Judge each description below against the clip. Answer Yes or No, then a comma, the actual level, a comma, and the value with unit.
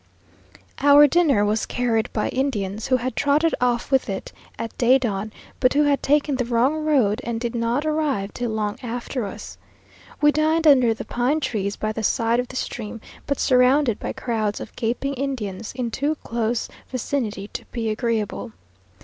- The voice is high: Yes, high, 245 Hz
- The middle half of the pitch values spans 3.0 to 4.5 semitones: Yes, average, 4.0 semitones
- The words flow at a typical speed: Yes, average, 175 wpm